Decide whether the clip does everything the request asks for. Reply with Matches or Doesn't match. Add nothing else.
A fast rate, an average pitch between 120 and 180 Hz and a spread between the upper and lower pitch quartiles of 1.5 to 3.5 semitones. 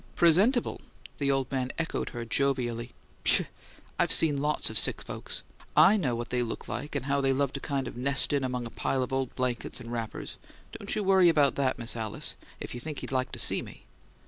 Matches